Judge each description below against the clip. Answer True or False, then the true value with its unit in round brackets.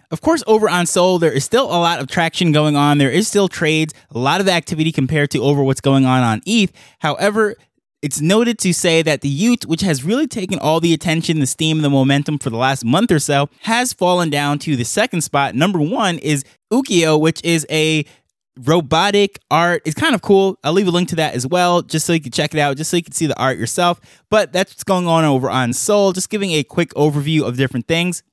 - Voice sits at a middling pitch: True (160 Hz)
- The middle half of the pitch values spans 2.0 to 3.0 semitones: False (4.0 semitones)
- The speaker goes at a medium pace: False (240 wpm)